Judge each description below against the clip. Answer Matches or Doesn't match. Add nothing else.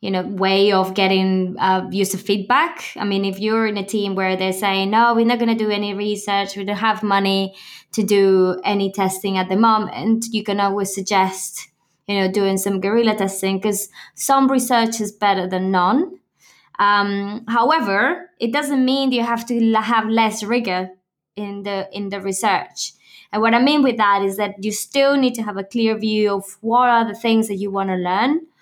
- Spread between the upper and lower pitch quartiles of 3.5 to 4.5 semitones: Doesn't match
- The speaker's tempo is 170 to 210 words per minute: Matches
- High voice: Matches